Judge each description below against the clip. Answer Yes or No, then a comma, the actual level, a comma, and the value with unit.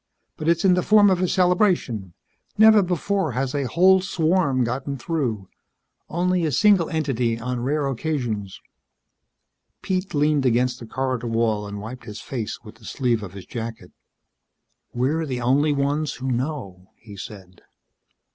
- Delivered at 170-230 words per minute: No, average, 155 wpm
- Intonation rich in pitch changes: Yes, wide, 6.2 semitones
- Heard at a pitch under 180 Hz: Yes, low, 135 Hz